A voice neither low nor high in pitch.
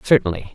No: low, 110 Hz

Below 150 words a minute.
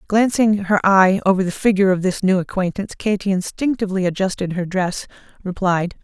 No: average, 160 wpm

